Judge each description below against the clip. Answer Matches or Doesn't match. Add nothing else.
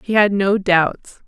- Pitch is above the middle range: Matches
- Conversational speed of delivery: Matches